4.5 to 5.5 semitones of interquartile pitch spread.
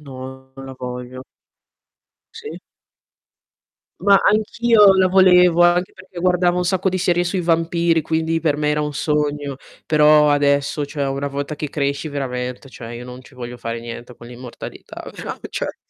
Yes: average, 4.9 semitones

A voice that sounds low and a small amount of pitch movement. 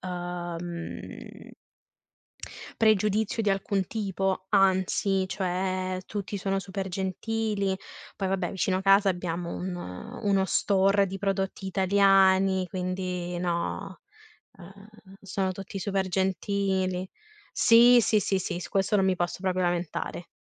No: high, 190 Hz; narrow, 1.4 semitones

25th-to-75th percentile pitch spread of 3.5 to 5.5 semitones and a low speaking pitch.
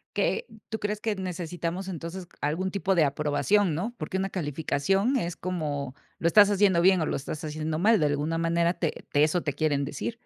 No: average, 4.0 semitones; medium, 170 Hz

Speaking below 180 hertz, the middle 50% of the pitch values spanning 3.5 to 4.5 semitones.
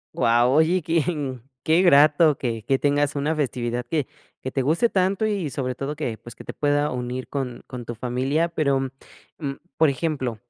Yes: medium, 140 Hz; average, 3.8 semitones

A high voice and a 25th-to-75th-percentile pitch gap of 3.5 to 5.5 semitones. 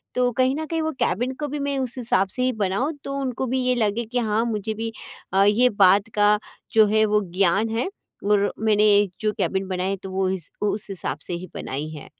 Yes: high, 215 Hz; average, 4.1 semitones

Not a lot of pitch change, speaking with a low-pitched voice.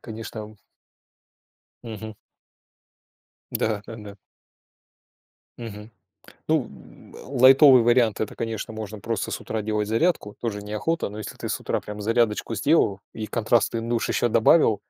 Yes: narrow, 2.0 semitones; low, 110 Hz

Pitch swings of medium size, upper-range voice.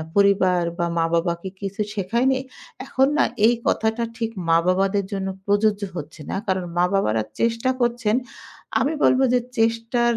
Yes: average, 4.1 semitones; high, 200 Hz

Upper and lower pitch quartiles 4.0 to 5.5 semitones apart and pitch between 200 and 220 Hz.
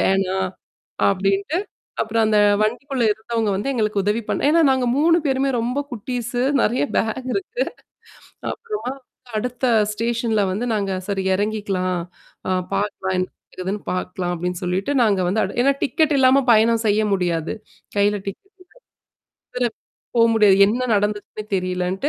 Yes: average, 4.4 semitones; high, 215 Hz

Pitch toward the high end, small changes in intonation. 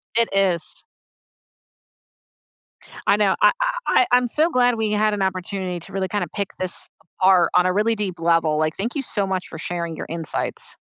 No: high, 195 Hz; average, 3.5 semitones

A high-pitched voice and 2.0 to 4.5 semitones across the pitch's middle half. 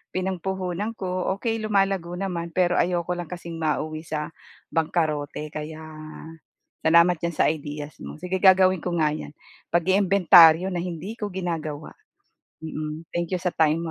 No: medium, 175 Hz; average, 2.9 semitones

